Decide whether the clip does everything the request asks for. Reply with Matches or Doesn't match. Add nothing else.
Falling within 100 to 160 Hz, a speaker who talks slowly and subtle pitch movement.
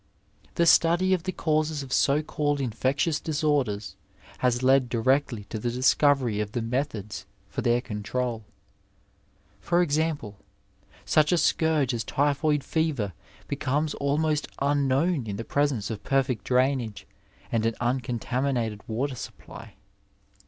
Doesn't match